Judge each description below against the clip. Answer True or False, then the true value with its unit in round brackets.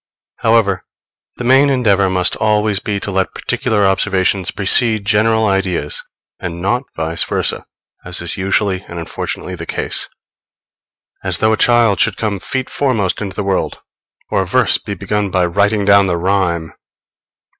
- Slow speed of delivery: False (155 wpm)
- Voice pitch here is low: True (100 Hz)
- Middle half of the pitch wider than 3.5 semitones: False (2.8 semitones)